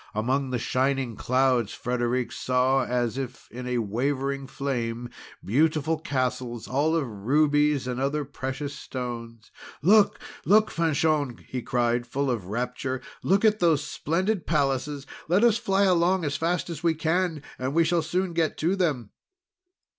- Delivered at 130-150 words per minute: Yes, average, 145 wpm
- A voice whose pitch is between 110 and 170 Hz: Yes, medium, 140 Hz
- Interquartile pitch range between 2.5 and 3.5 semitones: No, average, 4.5 semitones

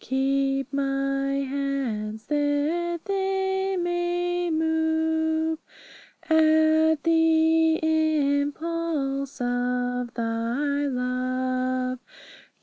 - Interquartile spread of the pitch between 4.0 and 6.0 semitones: No, average, 3.3 semitones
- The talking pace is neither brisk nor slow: No, slow, 60 wpm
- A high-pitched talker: Yes, very high, 290 Hz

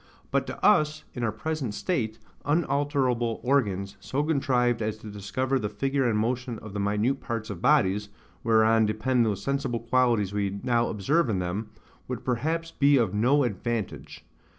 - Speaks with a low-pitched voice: Yes, low, 120 Hz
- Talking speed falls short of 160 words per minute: No, average, 165 wpm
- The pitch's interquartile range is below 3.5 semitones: No, average, 4.3 semitones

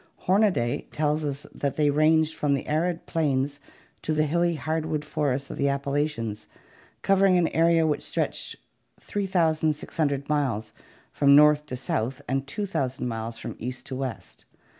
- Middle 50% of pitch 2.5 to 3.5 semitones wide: Yes, average, 2.8 semitones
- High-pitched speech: No, medium, 150 Hz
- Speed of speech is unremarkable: Yes, average, 150 wpm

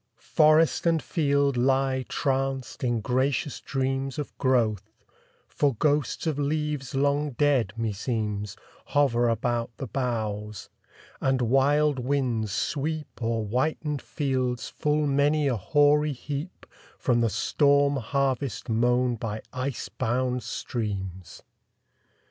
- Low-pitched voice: Yes, low, 130 Hz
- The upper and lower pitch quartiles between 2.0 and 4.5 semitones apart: Yes, average, 3.6 semitones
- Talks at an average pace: No, slow, 115 wpm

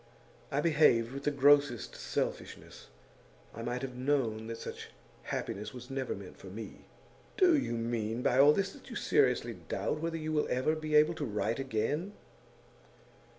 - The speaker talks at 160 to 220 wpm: Yes, average, 165 wpm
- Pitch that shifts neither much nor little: Yes, average, 4.8 semitones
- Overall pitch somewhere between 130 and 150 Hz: Yes, low, 135 Hz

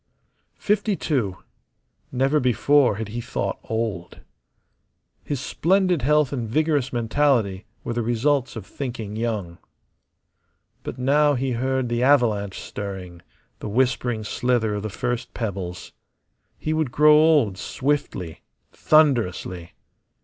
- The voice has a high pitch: No, low, 120 Hz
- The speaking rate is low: Yes, slow, 120 wpm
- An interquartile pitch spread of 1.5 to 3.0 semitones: No, wide, 5.4 semitones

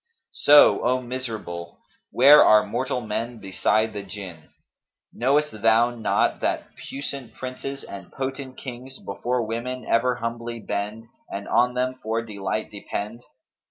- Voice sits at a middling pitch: No, low, 115 Hz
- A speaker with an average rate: No, slow, 130 wpm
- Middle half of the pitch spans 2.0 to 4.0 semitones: Yes, average, 3.2 semitones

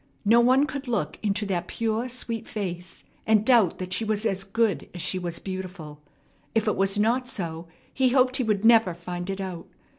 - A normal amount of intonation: Yes, average, 4.1 semitones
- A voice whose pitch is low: No, high, 205 Hz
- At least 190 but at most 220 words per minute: Yes, average, 200 wpm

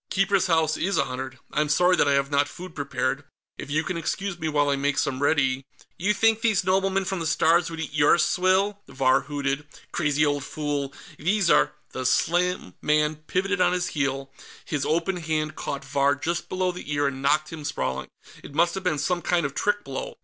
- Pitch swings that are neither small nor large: Yes, average, 4.2 semitones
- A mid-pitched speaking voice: Yes, medium, 155 Hz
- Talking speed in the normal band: No, fast, 210 wpm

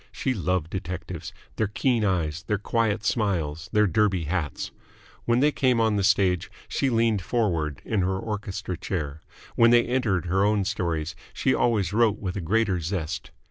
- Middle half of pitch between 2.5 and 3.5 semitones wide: No, average, 4.2 semitones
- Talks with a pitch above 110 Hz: No, low, 100 Hz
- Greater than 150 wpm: Yes, average, 170 wpm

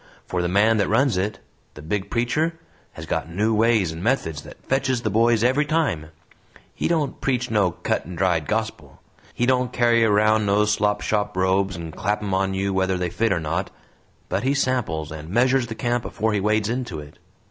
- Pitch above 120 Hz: No, low, 105 Hz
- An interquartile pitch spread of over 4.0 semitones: Yes, average, 4.4 semitones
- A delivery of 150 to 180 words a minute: No, average, 200 wpm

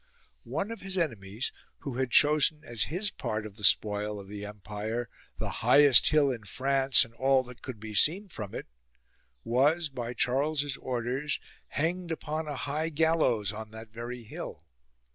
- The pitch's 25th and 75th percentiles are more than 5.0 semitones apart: Yes, wide, 5.5 semitones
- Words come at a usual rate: Yes, average, 165 wpm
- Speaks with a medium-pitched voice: No, low, 130 Hz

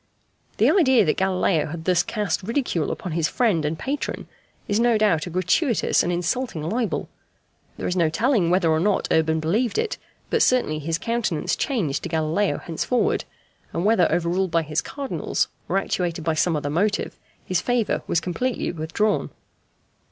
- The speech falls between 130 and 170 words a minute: Yes, average, 165 wpm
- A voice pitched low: No, medium, 180 Hz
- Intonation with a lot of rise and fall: Yes, wide, 5.9 semitones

